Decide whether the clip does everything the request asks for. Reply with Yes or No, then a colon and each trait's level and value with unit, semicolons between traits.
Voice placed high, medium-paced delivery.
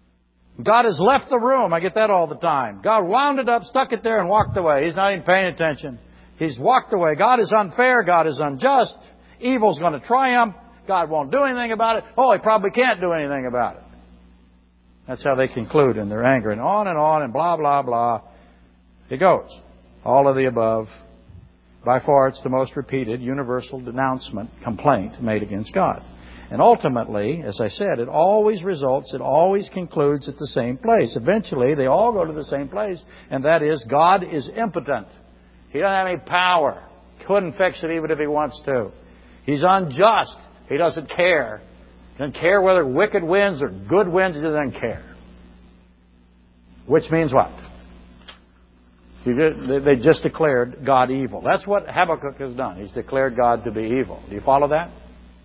No: medium, 140 Hz; average, 185 wpm